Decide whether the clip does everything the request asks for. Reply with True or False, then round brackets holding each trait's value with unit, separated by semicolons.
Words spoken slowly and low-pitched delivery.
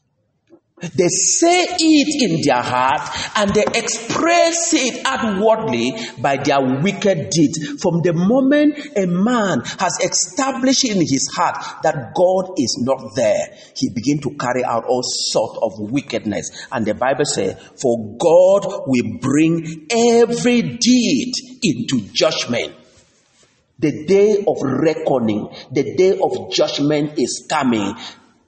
False (130 wpm; 190 Hz)